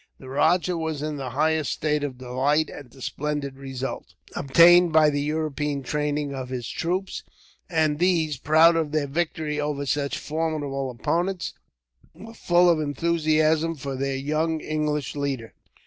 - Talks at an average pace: Yes, average, 150 wpm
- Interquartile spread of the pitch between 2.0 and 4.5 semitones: Yes, narrow, 2.5 semitones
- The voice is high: No, medium, 150 Hz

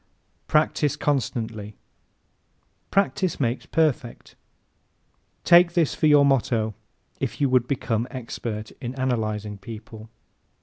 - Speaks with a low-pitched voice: Yes, low, 125 Hz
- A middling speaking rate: No, slow, 105 wpm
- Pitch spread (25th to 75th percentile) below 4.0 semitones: No, average, 4.8 semitones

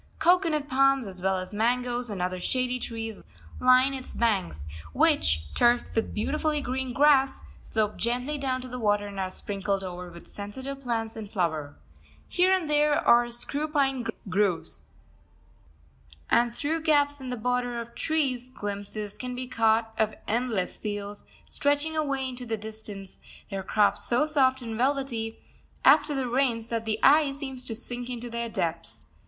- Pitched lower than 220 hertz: No, high, 240 Hz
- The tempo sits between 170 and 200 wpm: No, average, 160 wpm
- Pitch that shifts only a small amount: No, average, 4.4 semitones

